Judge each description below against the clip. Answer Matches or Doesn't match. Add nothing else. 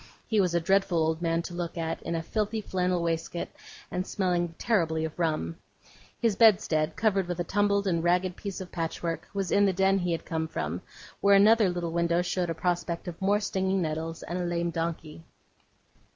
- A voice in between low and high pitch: Matches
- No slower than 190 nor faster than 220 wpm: Matches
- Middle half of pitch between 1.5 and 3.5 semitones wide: Matches